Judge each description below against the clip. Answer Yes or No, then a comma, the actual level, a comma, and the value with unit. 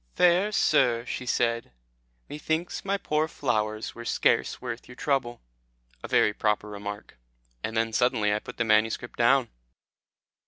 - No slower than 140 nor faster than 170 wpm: Yes, average, 145 wpm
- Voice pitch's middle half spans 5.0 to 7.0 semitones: No, average, 4.1 semitones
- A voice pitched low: Yes, low, 120 Hz